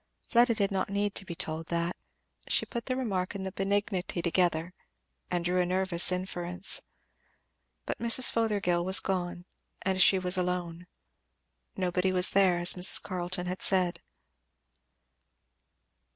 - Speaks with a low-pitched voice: No, medium, 185 Hz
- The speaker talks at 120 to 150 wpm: Yes, average, 140 wpm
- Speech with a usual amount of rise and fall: No, narrow, 1.7 semitones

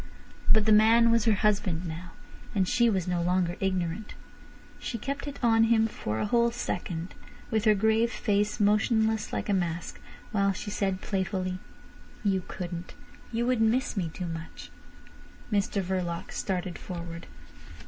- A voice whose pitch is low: No, high, 200 Hz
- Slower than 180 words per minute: Yes, average, 155 wpm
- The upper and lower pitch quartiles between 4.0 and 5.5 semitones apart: No, average, 3.6 semitones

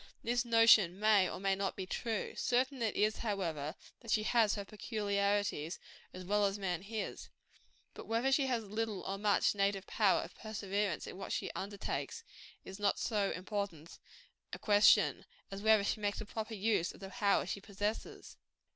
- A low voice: No, high, 205 Hz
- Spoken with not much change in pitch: Yes, narrow, 2.0 semitones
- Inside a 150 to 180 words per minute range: Yes, average, 175 wpm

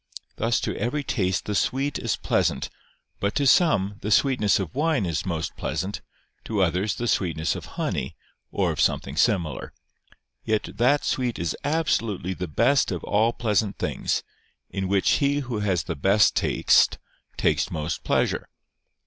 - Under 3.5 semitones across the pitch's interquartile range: No, average, 5.2 semitones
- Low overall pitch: Yes, low, 105 Hz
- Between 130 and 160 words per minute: Yes, average, 155 wpm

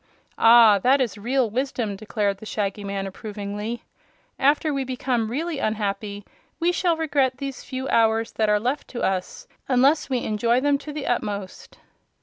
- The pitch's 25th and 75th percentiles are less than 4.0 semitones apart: No, average, 4.6 semitones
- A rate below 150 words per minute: No, average, 160 wpm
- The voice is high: Yes, high, 235 Hz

